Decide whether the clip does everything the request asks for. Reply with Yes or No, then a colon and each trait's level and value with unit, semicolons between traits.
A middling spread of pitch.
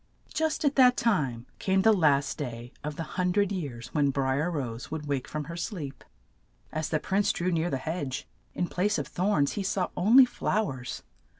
No: wide, 5.9 semitones